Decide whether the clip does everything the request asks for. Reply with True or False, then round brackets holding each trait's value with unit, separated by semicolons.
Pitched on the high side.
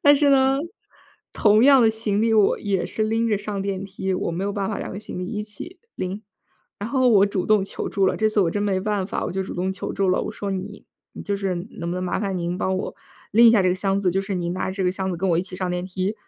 True (195 Hz)